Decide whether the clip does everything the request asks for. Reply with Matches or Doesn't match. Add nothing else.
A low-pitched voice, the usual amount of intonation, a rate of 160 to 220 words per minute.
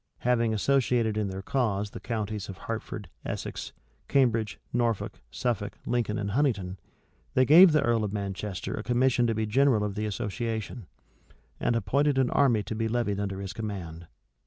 Matches